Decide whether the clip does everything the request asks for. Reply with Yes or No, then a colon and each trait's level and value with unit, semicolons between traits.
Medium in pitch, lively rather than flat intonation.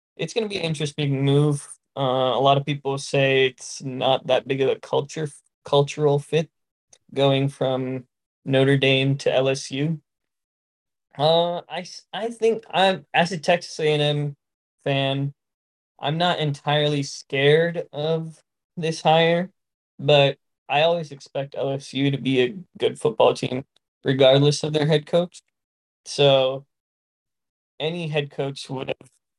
No: medium, 145 Hz; average, 3.0 semitones